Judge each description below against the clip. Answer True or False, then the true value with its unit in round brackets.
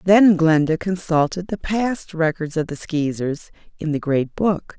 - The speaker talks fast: False (165 wpm)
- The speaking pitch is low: False (170 Hz)